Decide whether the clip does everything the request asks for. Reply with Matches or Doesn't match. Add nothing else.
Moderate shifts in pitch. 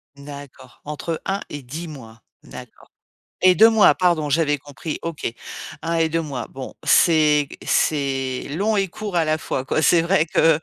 Matches